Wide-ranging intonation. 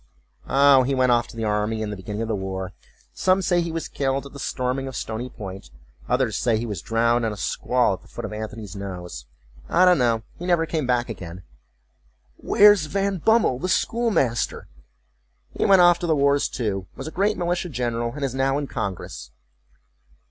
Yes: wide, 6.7 semitones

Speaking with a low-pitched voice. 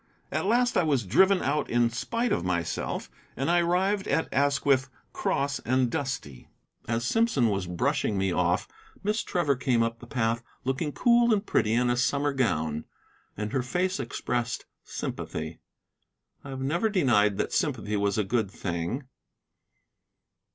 Yes: low, 130 Hz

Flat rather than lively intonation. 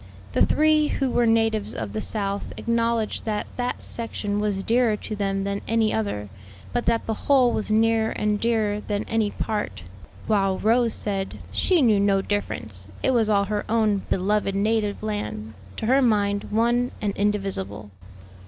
Yes: narrow, 2.3 semitones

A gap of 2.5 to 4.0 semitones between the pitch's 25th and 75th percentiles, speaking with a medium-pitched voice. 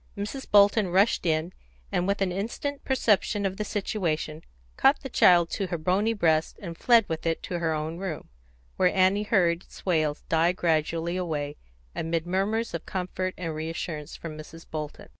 Yes: average, 3.6 semitones; medium, 180 Hz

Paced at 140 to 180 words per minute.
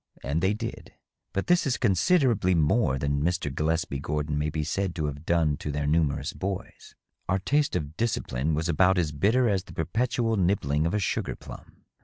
No: average, 190 wpm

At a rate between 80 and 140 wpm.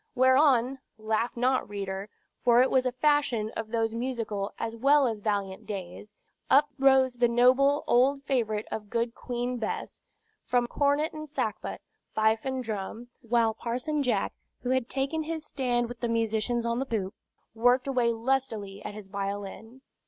No: average, 160 wpm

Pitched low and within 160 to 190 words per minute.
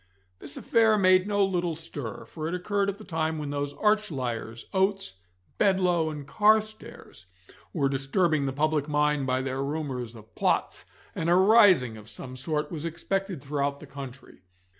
No: medium, 155 Hz; average, 165 wpm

